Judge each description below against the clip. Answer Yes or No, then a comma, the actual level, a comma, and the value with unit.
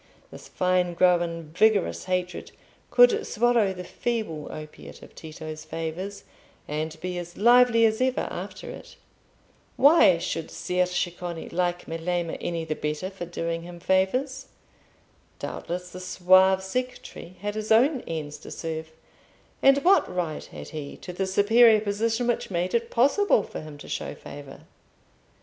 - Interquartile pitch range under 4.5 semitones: No, average, 4.9 semitones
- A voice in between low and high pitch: Yes, medium, 180 Hz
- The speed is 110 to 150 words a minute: Yes, average, 145 wpm